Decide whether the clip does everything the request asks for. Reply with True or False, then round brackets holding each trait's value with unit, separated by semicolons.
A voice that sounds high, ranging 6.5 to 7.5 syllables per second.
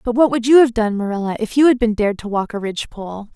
True (225 Hz; 6.9 syllables/s)